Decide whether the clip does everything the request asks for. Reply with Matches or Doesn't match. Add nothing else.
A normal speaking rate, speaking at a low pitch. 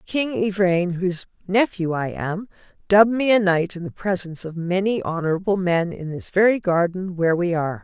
Doesn't match